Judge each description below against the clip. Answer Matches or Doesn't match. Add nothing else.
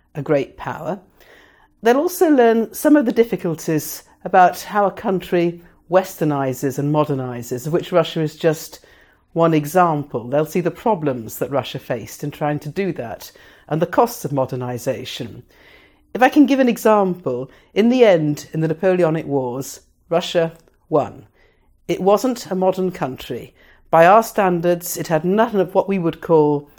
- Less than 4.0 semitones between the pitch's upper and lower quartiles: Doesn't match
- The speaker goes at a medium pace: Matches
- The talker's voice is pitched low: Doesn't match